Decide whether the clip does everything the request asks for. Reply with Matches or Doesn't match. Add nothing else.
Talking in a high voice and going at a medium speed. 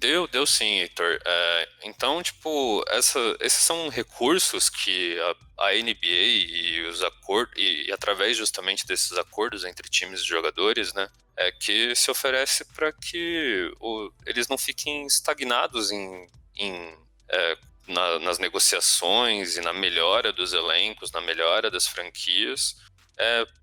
Doesn't match